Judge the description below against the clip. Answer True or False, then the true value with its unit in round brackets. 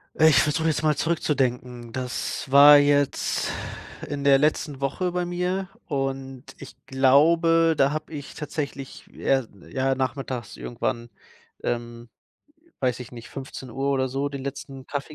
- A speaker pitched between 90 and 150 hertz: True (140 Hz)